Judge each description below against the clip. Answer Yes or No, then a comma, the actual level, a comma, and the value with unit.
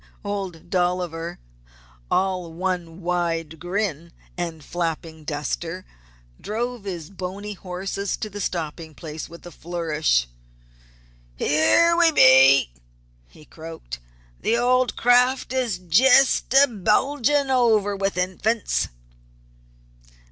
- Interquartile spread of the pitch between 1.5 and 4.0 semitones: No, average, 4.7 semitones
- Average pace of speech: No, slow, 105 wpm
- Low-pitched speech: No, medium, 180 Hz